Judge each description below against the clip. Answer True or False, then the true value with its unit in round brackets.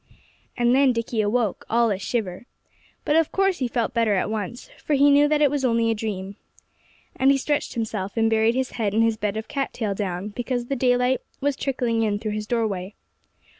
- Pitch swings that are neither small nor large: True (3.6 semitones)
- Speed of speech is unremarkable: False (210 wpm)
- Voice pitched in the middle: False (230 Hz)